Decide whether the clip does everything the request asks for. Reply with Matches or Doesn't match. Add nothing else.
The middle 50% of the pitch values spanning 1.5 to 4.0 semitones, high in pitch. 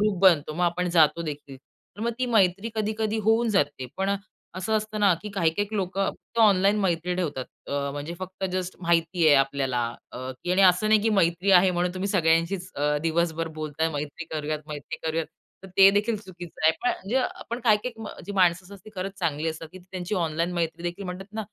Doesn't match